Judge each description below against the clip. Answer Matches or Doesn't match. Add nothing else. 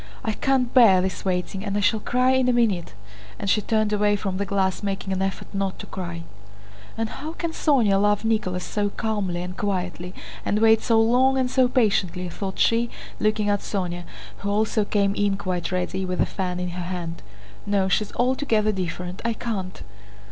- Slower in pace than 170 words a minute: Doesn't match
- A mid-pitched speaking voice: Doesn't match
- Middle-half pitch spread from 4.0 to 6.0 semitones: Doesn't match